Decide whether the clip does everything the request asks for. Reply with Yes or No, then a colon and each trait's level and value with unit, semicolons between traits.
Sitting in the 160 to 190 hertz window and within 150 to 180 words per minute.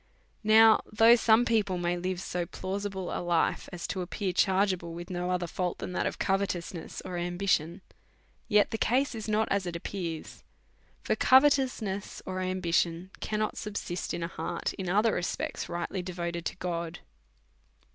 Yes: medium, 185 Hz; average, 170 wpm